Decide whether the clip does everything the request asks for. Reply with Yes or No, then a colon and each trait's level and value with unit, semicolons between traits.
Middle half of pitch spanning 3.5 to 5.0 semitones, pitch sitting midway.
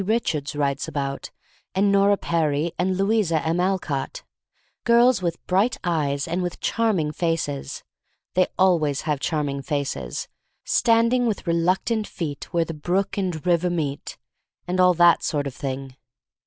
Yes: average, 4.6 semitones; medium, 170 Hz